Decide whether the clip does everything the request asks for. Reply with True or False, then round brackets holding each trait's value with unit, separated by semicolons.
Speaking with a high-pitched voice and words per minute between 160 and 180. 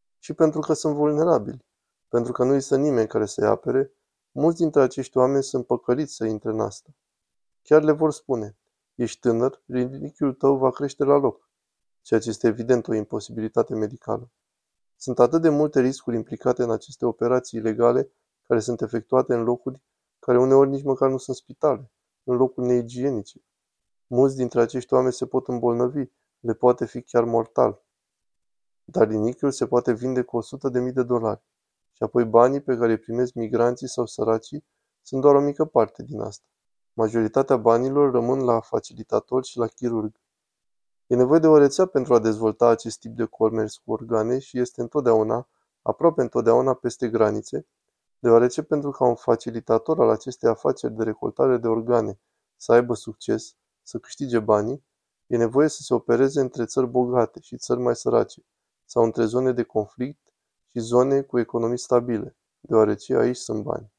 False (125 Hz; 170 wpm)